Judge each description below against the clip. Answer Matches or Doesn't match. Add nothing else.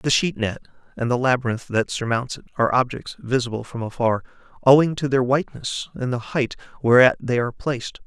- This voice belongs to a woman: Doesn't match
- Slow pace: Doesn't match